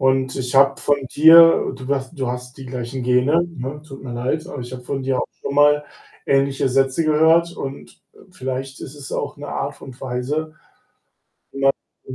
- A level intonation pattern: Yes, narrow, 2.2 semitones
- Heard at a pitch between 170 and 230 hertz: No, low, 135 Hz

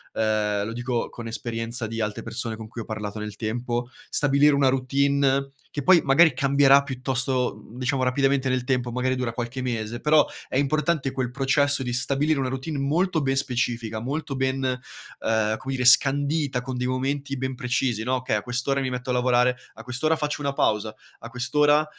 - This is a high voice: No, low, 130 Hz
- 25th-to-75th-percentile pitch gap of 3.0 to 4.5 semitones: No, narrow, 2.5 semitones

